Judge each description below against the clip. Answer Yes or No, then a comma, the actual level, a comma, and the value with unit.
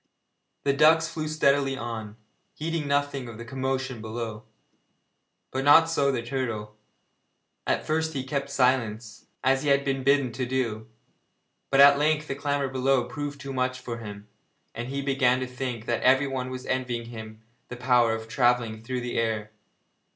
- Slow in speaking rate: No, average, 165 wpm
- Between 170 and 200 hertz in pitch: No, low, 130 Hz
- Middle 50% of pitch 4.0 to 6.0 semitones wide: No, average, 3.0 semitones